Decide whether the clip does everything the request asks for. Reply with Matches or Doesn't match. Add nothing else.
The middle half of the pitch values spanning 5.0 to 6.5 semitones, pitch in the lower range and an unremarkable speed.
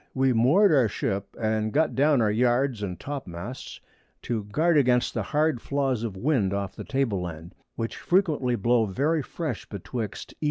Matches